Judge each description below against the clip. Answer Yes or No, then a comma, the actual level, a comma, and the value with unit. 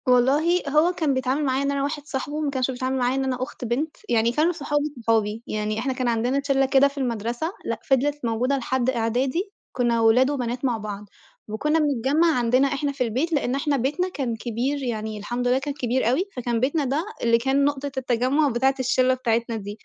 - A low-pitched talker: No, very high, 260 Hz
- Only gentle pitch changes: No, average, 3.0 semitones